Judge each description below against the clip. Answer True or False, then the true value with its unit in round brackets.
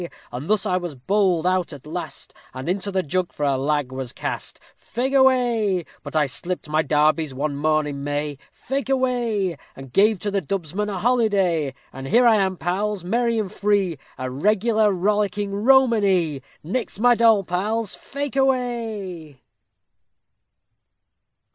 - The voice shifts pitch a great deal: True (6.2 semitones)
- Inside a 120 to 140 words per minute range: False (155 wpm)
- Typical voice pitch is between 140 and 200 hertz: True (190 Hz)